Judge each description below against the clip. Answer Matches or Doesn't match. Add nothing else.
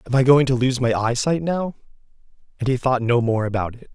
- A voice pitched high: Doesn't match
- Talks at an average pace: Doesn't match